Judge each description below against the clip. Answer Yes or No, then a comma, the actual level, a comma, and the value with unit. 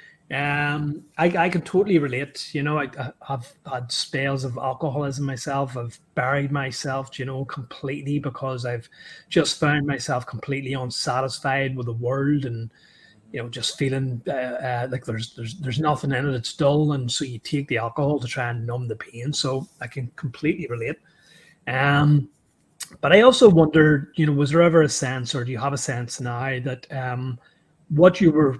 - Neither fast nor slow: Yes, average, 185 wpm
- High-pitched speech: No, low, 135 Hz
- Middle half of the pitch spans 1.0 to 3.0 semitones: Yes, average, 2.7 semitones